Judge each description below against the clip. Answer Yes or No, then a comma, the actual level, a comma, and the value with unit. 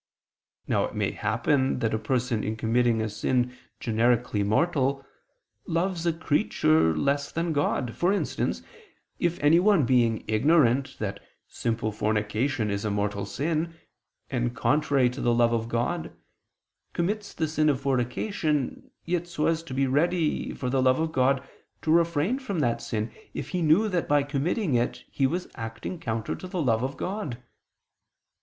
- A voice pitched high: No, low, 135 Hz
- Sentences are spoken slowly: No, average, 160 wpm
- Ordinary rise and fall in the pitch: No, wide, 6.0 semitones